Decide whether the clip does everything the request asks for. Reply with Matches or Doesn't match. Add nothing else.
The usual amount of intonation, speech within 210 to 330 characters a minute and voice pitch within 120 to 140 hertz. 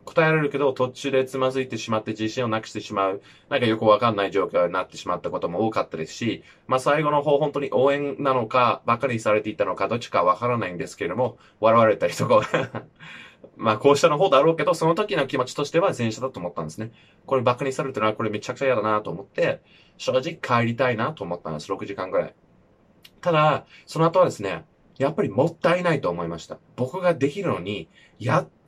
Doesn't match